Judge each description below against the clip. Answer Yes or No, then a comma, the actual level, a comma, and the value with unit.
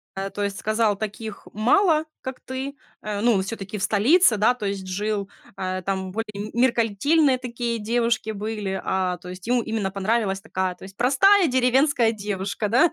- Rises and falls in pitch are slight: No, average, 3.7 semitones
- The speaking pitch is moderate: No, high, 215 Hz